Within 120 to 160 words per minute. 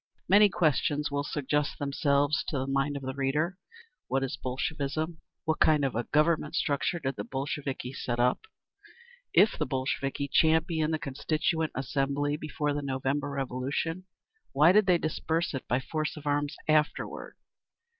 Yes: average, 155 wpm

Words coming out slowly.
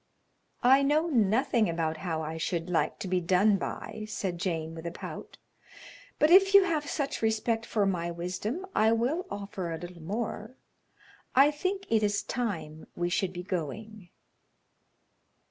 No: average, 160 wpm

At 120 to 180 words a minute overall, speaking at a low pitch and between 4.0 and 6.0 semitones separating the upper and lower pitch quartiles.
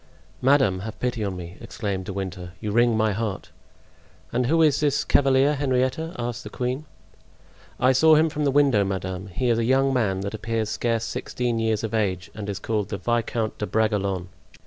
No: average, 190 wpm; low, 115 Hz; average, 4.6 semitones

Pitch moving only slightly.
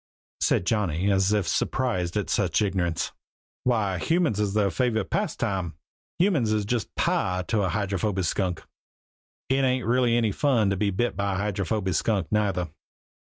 No: average, 3.4 semitones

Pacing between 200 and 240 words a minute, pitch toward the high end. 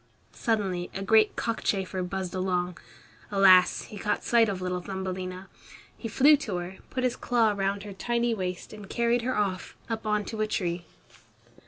No: average, 170 wpm; high, 195 Hz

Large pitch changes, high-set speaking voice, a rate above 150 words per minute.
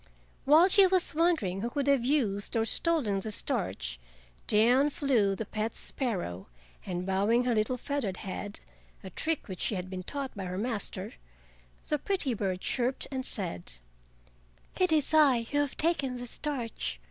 Yes: wide, 6.7 semitones; high, 230 Hz; average, 160 wpm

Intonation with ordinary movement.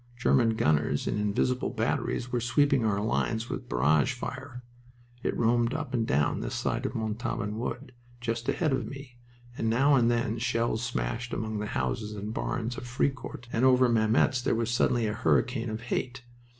No: narrow, 2.3 semitones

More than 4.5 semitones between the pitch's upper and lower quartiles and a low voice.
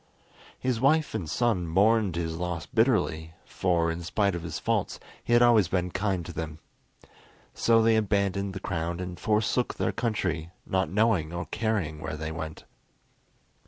Yes: average, 4.9 semitones; very low, 95 Hz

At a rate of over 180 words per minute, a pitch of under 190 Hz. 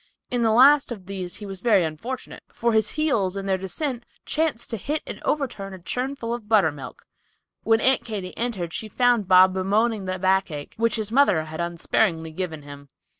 No: average, 190 wpm; high, 205 Hz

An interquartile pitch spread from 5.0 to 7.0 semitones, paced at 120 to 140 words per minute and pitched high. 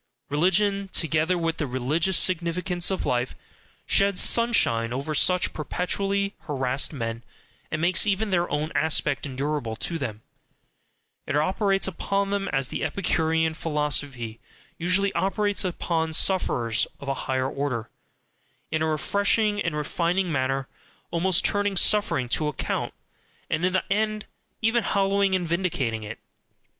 No: wide, 5.5 semitones; slow, 135 wpm; medium, 165 Hz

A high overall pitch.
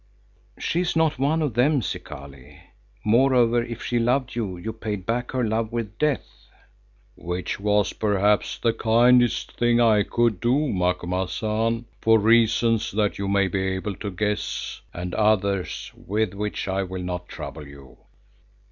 No: low, 110 Hz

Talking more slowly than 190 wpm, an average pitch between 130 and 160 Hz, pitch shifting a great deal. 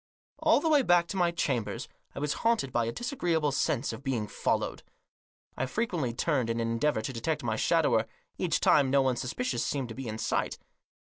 No: average, 200 wpm; low, 135 Hz; wide, 6.3 semitones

